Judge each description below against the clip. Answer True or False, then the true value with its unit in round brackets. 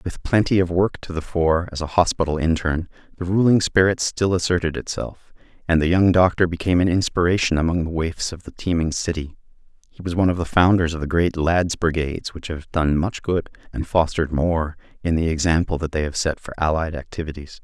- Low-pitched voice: True (85 Hz)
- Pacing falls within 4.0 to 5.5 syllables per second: False (5.8 syllables/s)